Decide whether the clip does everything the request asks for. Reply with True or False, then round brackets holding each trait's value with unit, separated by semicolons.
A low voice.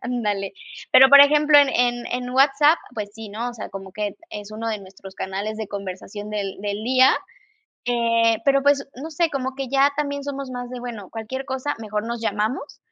False (240 Hz)